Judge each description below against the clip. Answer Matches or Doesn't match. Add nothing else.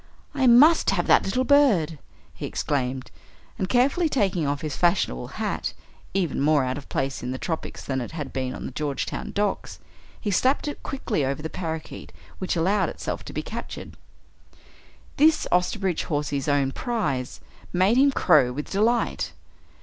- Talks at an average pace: Matches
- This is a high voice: Doesn't match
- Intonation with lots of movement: Matches